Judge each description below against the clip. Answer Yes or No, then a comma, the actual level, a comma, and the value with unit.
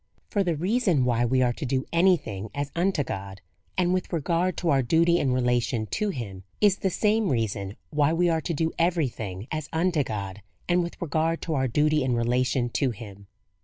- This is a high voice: No, medium, 145 Hz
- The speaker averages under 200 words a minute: No, fast, 205 wpm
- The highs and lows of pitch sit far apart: Yes, wide, 6.2 semitones